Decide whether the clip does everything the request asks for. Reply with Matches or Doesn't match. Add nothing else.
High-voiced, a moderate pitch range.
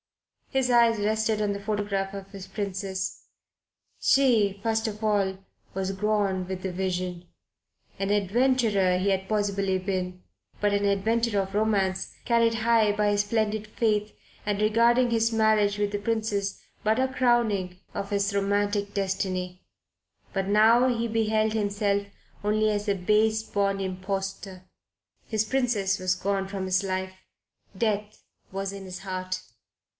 Doesn't match